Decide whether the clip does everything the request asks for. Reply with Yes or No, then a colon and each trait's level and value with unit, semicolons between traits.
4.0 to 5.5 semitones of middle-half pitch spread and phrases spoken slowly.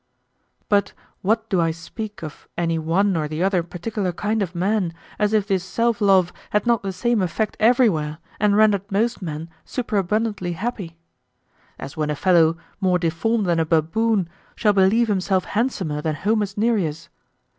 No: average, 4.3 semitones; average, 165 wpm